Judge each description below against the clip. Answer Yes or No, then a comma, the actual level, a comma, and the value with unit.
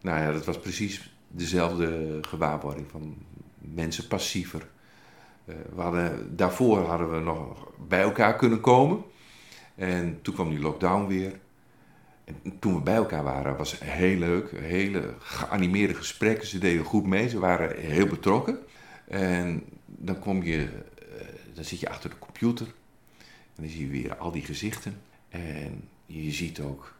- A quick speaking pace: No, average, 155 wpm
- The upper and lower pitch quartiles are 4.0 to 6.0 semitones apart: Yes, average, 4.3 semitones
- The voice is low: Yes, very low, 90 Hz